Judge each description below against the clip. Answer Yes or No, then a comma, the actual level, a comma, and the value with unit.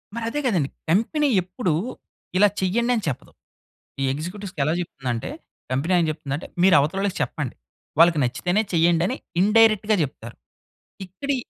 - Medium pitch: Yes, medium, 180 Hz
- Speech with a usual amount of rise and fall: No, wide, 5.7 semitones